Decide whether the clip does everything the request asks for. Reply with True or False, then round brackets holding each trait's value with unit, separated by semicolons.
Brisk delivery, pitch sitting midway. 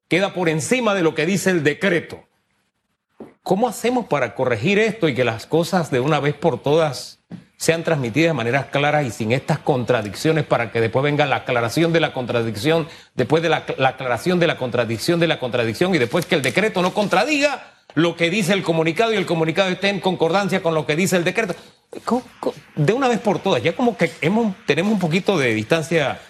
True (205 wpm; 165 Hz)